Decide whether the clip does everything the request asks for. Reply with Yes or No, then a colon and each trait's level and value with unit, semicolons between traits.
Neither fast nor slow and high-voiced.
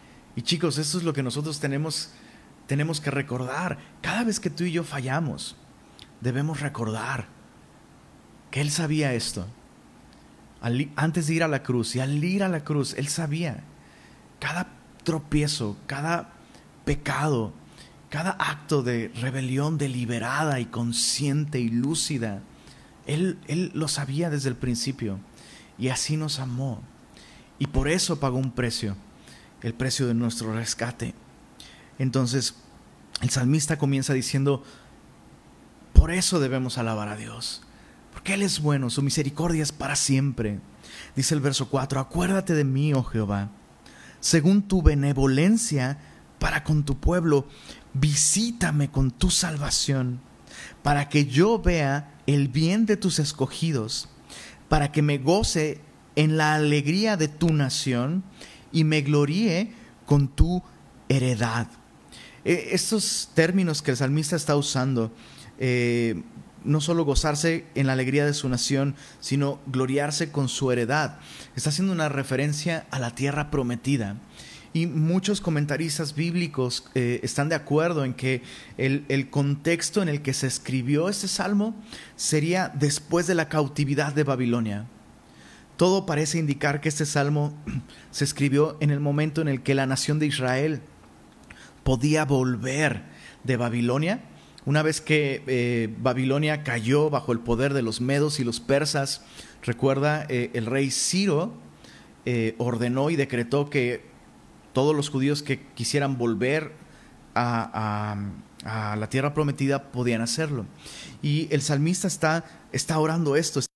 No: average, 140 wpm; medium, 140 Hz